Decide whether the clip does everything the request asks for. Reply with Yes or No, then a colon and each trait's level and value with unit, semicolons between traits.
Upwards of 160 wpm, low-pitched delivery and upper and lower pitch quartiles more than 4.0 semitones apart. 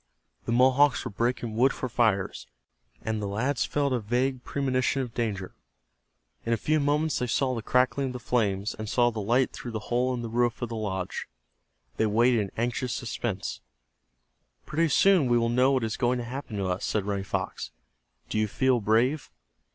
No: average, 195 wpm; low, 120 Hz; average, 3.0 semitones